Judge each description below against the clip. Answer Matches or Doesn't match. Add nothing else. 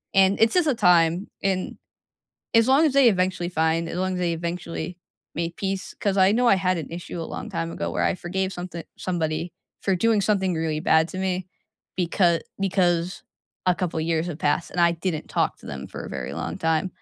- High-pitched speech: Doesn't match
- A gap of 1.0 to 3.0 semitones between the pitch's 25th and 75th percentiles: Matches